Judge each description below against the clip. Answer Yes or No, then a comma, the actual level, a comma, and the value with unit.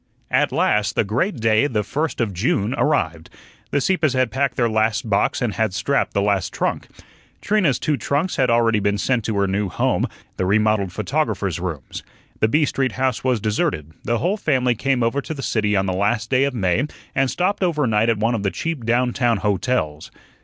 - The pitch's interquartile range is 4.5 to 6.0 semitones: Yes, average, 4.8 semitones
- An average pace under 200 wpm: No, fast, 205 wpm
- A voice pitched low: Yes, low, 115 Hz